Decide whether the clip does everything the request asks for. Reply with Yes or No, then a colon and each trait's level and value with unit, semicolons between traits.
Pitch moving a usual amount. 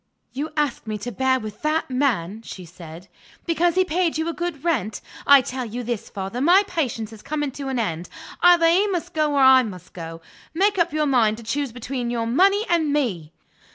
No: wide, 6.6 semitones